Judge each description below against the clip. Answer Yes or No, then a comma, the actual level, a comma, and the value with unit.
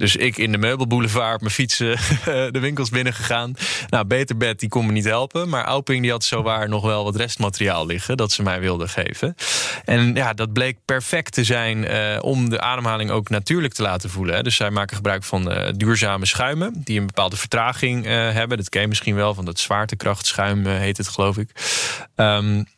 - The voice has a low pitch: Yes, low, 110 Hz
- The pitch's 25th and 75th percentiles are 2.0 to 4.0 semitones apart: Yes, average, 3.2 semitones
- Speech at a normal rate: No, fast, 205 wpm